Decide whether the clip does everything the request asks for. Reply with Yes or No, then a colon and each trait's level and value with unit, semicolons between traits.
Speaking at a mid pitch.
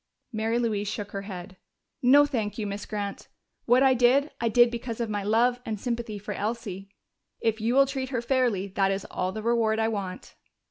No: high, 225 Hz